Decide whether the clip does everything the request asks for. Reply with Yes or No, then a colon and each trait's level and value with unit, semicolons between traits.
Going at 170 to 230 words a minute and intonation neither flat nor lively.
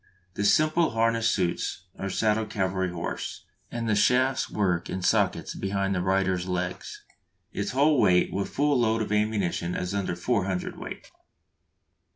No: average, 150 wpm; average, 3.8 semitones